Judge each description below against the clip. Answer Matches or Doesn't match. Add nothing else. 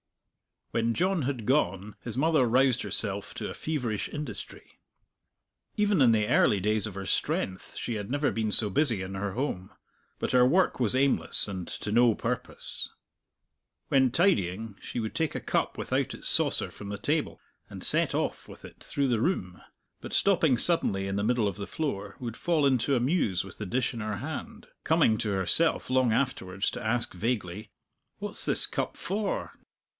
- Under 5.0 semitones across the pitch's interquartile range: Doesn't match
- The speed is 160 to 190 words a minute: Matches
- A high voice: Doesn't match